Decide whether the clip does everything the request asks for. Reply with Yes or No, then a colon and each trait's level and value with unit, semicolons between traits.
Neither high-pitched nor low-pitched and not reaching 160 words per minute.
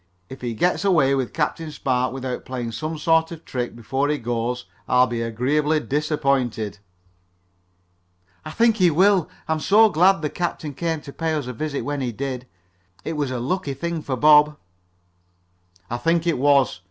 No: medium, 145 Hz; average, 175 wpm